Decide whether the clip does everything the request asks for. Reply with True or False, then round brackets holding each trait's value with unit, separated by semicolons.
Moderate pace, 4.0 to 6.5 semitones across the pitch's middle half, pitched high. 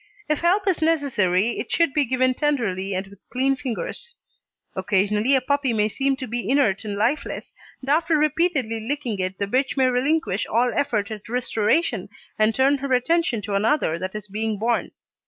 True (180 wpm; 5.3 semitones; 250 Hz)